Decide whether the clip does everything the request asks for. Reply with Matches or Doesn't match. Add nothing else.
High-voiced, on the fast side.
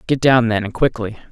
Doesn't match